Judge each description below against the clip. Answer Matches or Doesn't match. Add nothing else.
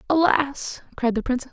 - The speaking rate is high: Doesn't match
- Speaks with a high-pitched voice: Matches